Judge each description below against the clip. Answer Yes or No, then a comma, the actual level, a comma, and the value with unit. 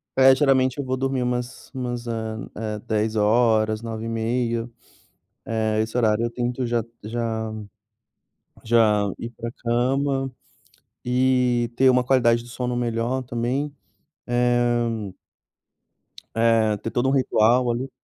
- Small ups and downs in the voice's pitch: Yes, narrow, 1.9 semitones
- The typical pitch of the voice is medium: No, low, 120 Hz